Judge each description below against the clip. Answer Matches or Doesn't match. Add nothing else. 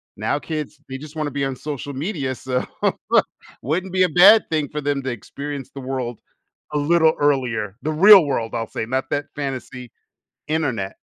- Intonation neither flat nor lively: Matches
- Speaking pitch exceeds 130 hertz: Matches